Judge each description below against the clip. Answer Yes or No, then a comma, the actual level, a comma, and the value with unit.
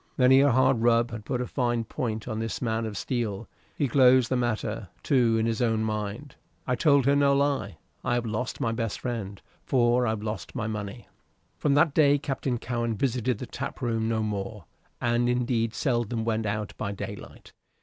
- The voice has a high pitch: No, low, 120 Hz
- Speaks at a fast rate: No, average, 190 wpm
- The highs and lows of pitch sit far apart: No, narrow, 2.5 semitones